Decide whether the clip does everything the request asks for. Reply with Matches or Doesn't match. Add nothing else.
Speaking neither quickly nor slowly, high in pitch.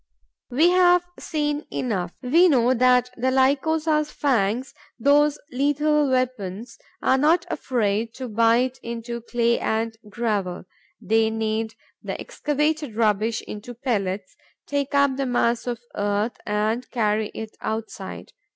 Doesn't match